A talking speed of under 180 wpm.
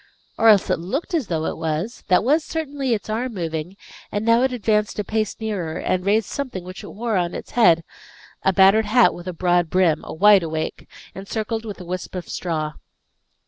No: fast, 205 wpm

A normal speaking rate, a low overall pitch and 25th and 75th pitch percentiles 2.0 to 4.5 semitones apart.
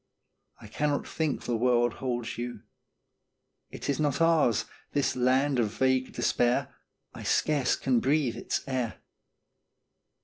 No: slow, 130 wpm; low, 130 Hz; average, 2.8 semitones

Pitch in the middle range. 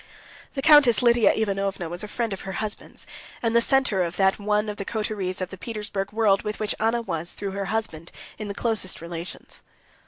No: high, 205 Hz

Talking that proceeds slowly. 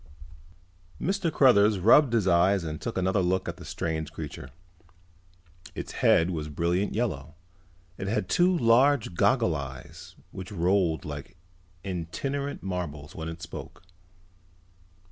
Yes: slow, 130 wpm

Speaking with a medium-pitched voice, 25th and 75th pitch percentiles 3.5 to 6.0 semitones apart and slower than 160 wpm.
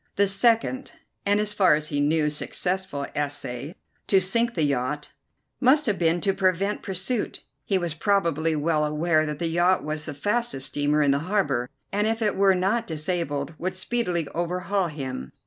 No: medium, 175 Hz; average, 4.8 semitones; average, 175 wpm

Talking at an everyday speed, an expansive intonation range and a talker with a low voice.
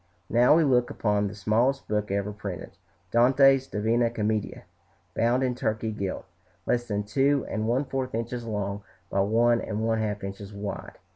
No: average, 165 wpm; average, 3.0 semitones; low, 110 Hz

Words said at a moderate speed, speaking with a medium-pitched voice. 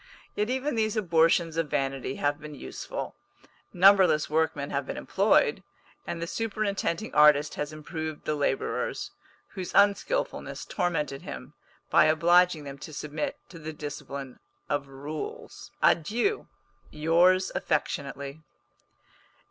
No: slow, 120 wpm; medium, 155 Hz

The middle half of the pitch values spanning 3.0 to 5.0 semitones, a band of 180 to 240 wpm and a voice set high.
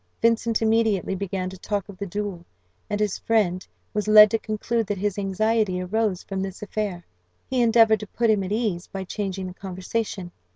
No: narrow, 2.6 semitones; average, 190 wpm; high, 205 Hz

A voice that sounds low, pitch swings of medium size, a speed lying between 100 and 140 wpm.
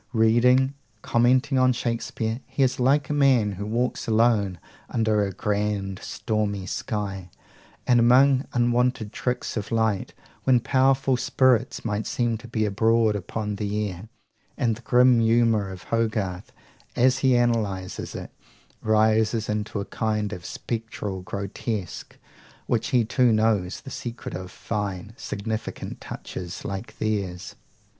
Yes: low, 110 Hz; average, 3.0 semitones; slow, 135 wpm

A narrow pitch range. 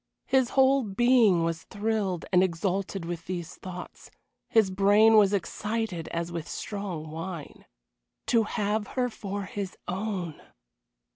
No: average, 3.9 semitones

